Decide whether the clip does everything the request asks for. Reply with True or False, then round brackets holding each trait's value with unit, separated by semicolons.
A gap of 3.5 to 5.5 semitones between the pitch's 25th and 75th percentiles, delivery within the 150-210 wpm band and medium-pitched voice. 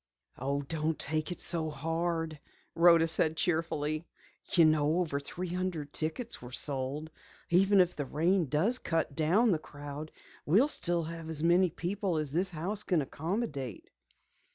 False (2.9 semitones; 155 wpm; 160 Hz)